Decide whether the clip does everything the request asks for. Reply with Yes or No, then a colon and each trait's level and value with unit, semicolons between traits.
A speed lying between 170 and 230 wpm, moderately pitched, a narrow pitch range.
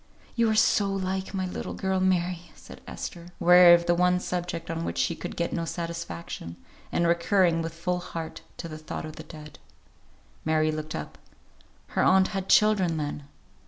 Yes: average, 180 wpm; medium, 170 Hz; narrow, 2.3 semitones